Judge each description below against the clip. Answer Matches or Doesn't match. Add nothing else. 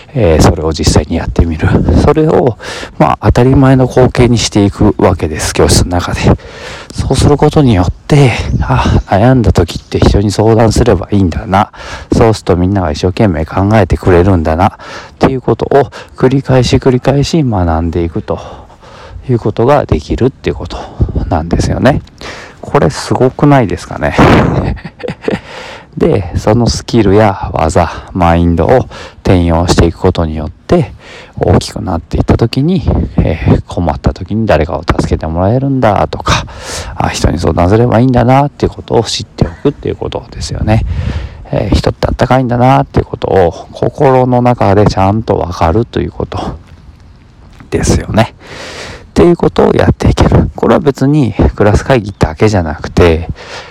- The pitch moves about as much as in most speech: Doesn't match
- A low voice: Matches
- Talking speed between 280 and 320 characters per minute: Doesn't match